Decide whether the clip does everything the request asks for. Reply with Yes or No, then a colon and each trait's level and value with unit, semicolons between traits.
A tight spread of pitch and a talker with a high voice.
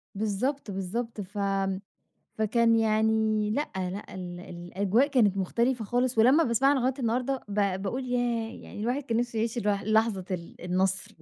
No: average, 3.6 semitones; high, 220 Hz